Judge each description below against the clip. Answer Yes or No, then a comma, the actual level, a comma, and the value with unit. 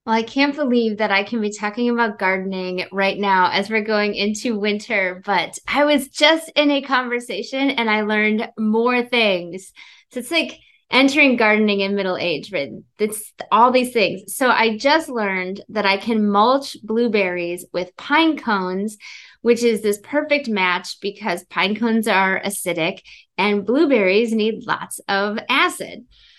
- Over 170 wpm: No, average, 160 wpm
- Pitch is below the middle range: No, high, 215 Hz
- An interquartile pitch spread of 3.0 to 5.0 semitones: Yes, average, 3.9 semitones